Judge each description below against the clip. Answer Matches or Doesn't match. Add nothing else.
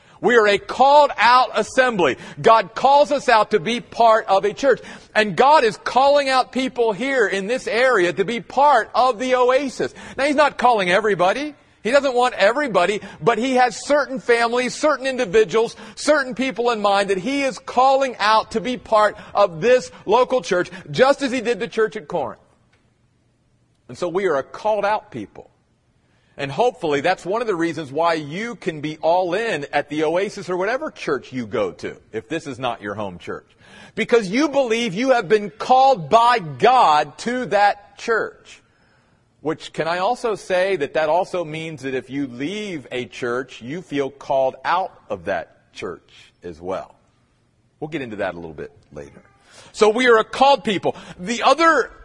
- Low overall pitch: Doesn't match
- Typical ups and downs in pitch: Doesn't match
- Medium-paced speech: Matches